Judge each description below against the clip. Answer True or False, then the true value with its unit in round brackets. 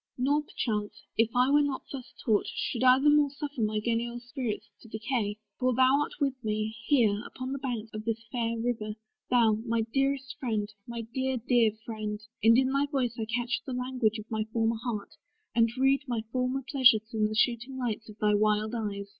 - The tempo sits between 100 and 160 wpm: False (200 wpm)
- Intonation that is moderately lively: True (3.1 semitones)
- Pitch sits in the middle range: False (235 Hz)